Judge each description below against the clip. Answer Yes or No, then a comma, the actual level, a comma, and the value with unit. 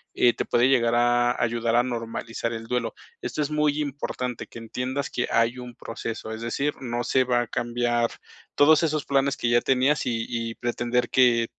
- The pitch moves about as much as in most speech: No, narrow, 1.9 semitones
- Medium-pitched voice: No, low, 120 Hz